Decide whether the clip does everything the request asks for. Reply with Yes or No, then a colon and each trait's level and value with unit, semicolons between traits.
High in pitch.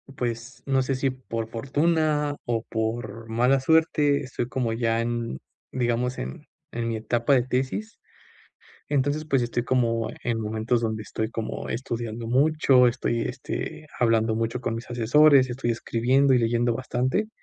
No: low, 120 Hz